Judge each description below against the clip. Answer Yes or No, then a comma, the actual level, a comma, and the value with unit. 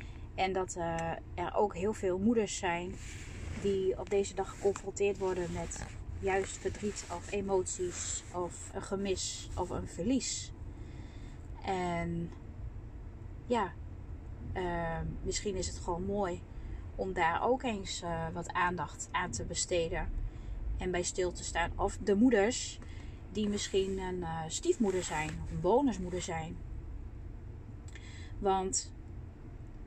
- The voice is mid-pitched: Yes, medium, 170 Hz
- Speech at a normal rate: No, slow, 125 wpm